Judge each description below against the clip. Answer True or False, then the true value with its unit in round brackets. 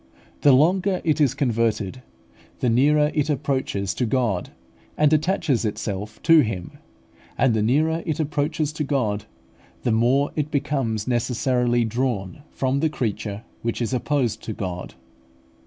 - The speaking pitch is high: False (130 Hz)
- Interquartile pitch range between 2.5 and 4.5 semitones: False (5.1 semitones)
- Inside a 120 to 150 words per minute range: True (140 wpm)